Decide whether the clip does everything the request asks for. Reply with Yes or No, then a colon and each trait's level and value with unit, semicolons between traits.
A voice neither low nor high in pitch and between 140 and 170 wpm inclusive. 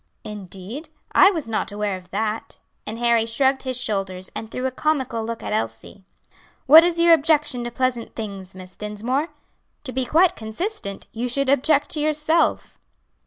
No: high, 240 Hz; average, 165 wpm